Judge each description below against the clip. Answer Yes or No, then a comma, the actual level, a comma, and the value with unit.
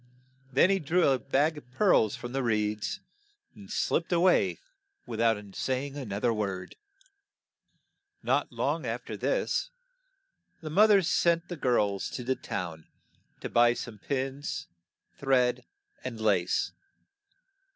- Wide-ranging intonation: Yes, wide, 6.7 semitones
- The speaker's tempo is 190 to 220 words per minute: No, average, 145 wpm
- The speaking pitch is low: Yes, low, 130 Hz